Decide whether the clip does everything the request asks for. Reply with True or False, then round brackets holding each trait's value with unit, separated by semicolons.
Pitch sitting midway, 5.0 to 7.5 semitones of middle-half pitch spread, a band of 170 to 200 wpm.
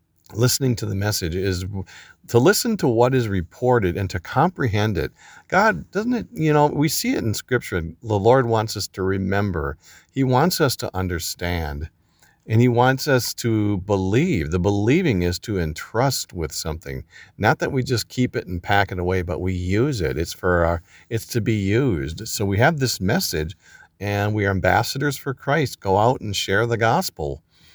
False (105 Hz; 5.5 semitones; 190 wpm)